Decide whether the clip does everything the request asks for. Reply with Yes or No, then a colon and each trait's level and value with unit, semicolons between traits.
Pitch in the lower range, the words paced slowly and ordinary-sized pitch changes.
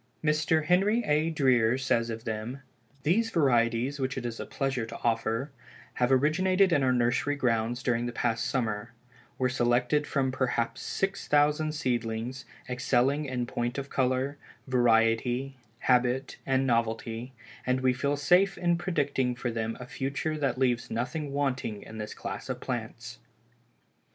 No: low, 130 Hz; average, 150 wpm; average, 3.4 semitones